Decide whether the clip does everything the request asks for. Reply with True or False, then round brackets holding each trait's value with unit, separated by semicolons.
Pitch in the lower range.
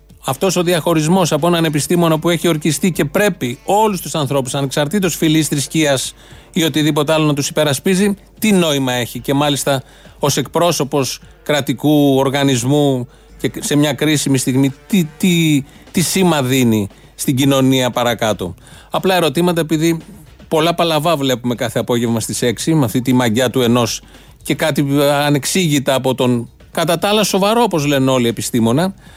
False (145 Hz)